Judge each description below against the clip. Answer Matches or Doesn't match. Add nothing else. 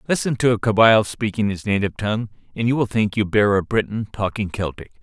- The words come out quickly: Matches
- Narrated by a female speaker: Doesn't match